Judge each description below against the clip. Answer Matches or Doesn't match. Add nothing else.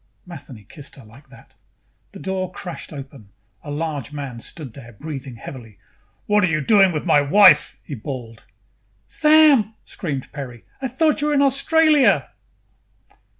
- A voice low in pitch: Doesn't match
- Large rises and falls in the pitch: Matches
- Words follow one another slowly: Doesn't match